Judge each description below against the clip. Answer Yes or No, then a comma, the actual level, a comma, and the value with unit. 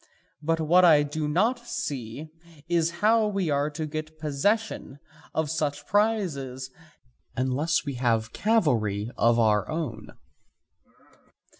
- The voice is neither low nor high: Yes, medium, 155 Hz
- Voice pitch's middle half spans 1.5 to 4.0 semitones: No, average, 4.8 semitones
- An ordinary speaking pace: No, slow, 120 wpm